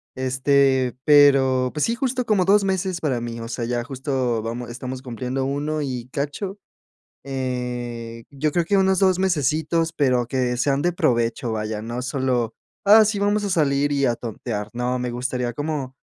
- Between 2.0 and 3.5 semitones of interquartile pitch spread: No, average, 4.1 semitones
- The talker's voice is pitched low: Yes, low, 130 Hz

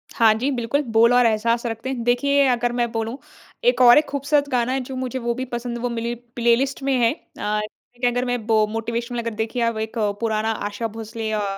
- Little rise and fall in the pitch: Yes, narrow, 2.0 semitones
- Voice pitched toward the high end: Yes, high, 235 Hz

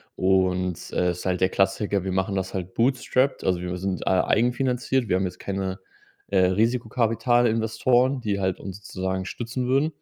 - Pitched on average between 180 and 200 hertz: No, low, 100 Hz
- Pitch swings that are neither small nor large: Yes, average, 4.5 semitones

